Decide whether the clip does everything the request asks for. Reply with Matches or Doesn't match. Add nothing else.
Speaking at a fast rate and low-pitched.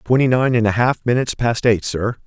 Matches